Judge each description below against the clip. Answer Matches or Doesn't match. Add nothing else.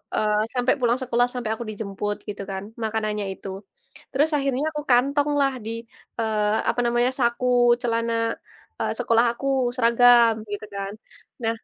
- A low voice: Doesn't match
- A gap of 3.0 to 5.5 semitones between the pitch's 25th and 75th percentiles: Doesn't match